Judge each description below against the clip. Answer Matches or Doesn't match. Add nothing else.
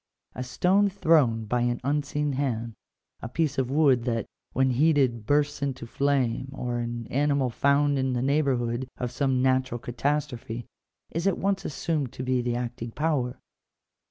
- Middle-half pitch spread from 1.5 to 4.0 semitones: Matches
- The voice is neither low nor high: Doesn't match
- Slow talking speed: Doesn't match